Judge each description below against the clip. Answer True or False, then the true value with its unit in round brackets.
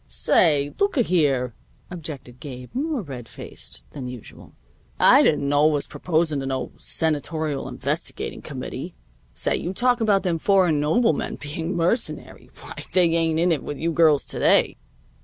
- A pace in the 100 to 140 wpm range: False (155 wpm)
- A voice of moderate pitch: True (160 Hz)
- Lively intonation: False (4.0 semitones)